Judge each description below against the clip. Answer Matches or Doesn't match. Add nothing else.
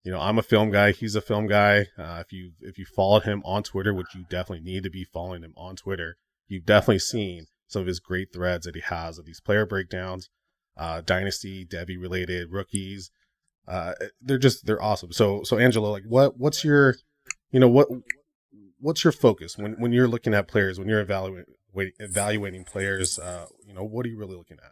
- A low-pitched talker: Matches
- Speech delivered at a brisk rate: Matches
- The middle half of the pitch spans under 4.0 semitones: Matches